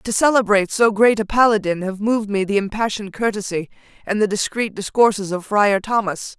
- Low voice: No, high, 210 Hz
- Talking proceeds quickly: No, average, 180 wpm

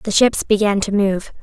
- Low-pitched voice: No, high, 205 Hz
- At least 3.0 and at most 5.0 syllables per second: Yes, 4.6 syllables/s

